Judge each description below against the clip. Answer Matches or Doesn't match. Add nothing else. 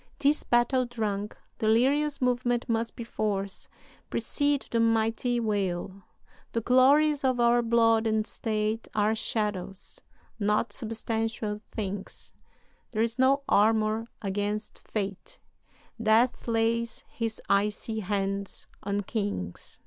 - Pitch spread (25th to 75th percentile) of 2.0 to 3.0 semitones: Matches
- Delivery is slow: Matches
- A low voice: Doesn't match